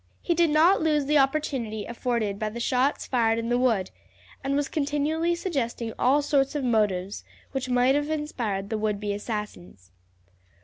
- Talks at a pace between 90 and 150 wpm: No, average, 170 wpm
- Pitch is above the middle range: Yes, very high, 250 Hz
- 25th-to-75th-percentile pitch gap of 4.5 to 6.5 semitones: Yes, average, 5.2 semitones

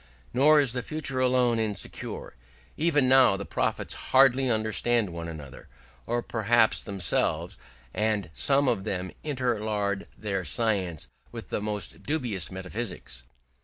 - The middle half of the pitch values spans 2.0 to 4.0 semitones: No, average, 4.8 semitones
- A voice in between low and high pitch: No, low, 110 Hz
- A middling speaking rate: No, slow, 130 wpm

